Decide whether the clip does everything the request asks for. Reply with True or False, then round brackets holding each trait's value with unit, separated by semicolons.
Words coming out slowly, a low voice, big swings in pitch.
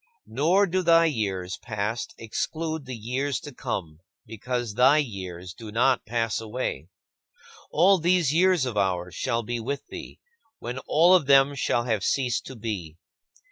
False (155 wpm; 125 Hz; 5.7 semitones)